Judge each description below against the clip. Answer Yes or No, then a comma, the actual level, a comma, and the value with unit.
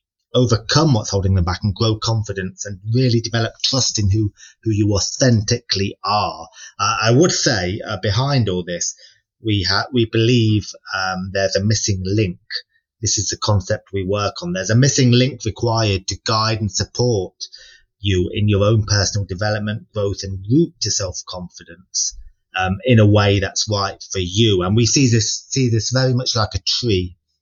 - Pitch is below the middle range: Yes, low, 105 Hz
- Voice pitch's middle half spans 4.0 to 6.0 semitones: No, average, 3.1 semitones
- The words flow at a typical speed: Yes, average, 175 wpm